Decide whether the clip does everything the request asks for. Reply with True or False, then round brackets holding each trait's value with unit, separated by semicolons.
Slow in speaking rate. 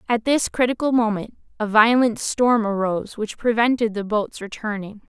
False (150 wpm)